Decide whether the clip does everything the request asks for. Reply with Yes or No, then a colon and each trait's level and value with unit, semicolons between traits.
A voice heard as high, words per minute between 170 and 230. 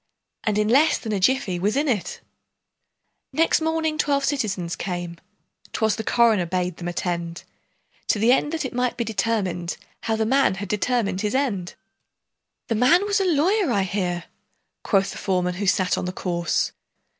Yes: high, 210 Hz; average, 175 wpm